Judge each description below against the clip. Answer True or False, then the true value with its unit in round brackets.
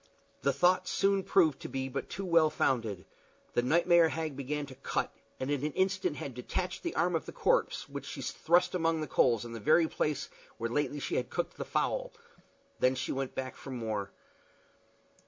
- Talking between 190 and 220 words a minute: True (195 wpm)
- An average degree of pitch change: True (5.0 semitones)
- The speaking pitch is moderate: True (145 Hz)